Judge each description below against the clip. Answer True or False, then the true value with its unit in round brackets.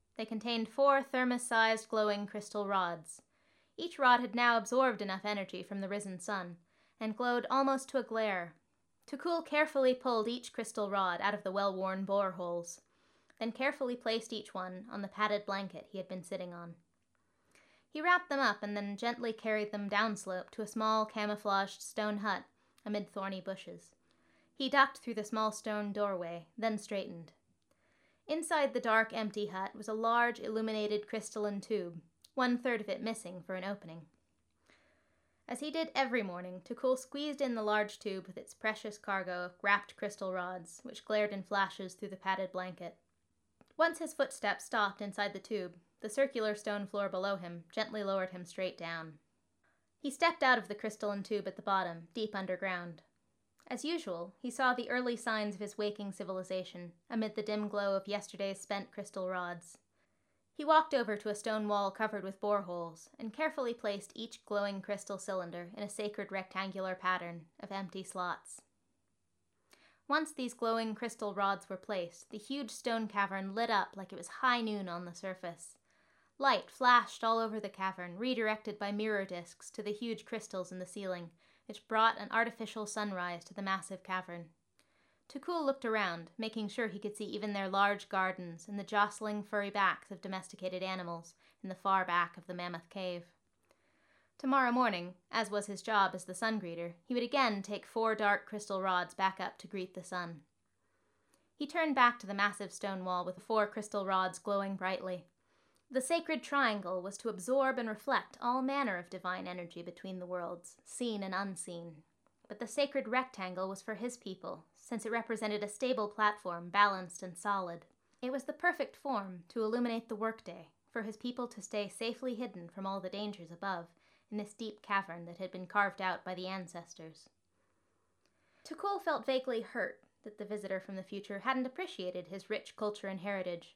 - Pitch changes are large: False (3.4 semitones)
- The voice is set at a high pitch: True (205 Hz)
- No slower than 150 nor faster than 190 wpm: True (180 wpm)